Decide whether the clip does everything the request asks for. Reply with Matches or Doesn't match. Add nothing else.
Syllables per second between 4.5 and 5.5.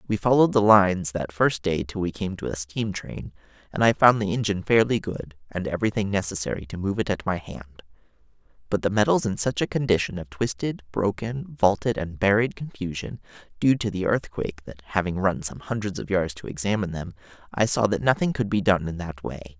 Doesn't match